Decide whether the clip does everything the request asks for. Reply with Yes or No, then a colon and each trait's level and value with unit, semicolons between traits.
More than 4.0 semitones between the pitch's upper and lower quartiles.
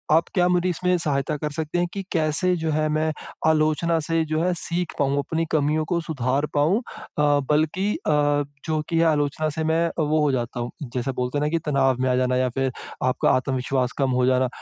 No: average, 3.5 semitones